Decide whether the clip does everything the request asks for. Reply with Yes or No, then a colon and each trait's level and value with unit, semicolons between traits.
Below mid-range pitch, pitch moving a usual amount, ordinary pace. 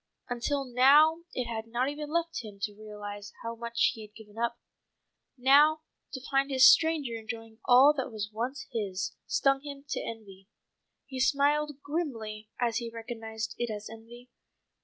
No: high, 240 Hz; average, 3.9 semitones; average, 165 wpm